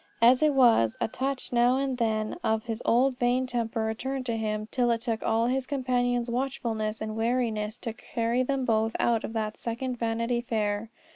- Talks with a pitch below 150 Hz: No, high, 235 Hz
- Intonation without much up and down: Yes, narrow, 2.2 semitones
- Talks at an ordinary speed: Yes, average, 190 wpm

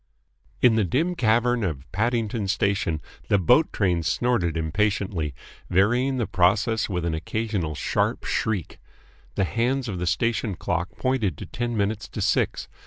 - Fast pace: No, average, 150 wpm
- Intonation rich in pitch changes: No, average, 5.0 semitones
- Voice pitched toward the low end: Yes, low, 105 Hz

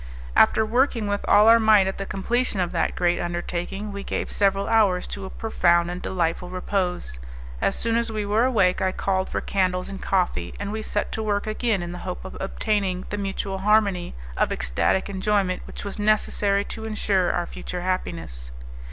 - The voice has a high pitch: Yes, high, 195 Hz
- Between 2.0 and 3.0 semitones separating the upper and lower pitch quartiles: Yes, average, 2.7 semitones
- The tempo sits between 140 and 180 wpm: No, average, 190 wpm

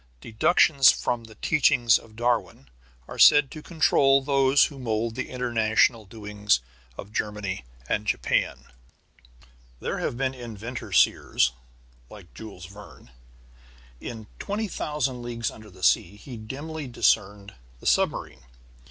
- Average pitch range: Yes, average, 4.5 semitones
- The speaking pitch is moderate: No, low, 115 Hz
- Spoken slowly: Yes, slow, 125 wpm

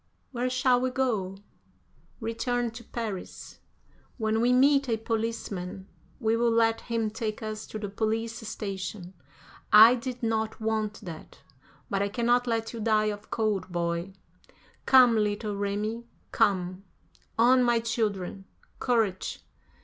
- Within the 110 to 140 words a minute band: Yes, slow, 135 wpm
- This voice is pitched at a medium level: No, high, 220 Hz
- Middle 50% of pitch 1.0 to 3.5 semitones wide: Yes, narrow, 2.4 semitones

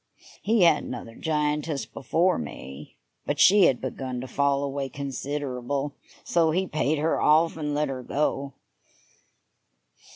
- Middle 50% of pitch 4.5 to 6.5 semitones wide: No, average, 2.8 semitones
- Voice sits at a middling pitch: Yes, medium, 145 Hz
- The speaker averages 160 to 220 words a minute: No, slow, 135 wpm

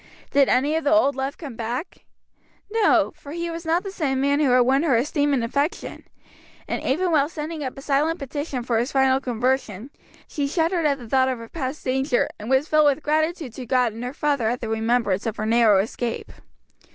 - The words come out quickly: Yes, fast, 210 wpm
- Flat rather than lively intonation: No, average, 3.9 semitones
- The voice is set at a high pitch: Yes, very high, 275 Hz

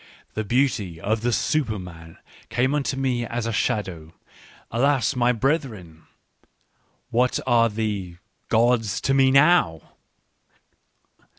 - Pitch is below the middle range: Yes, low, 115 Hz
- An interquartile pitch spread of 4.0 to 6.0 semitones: Yes, average, 4.8 semitones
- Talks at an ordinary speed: No, slow, 115 wpm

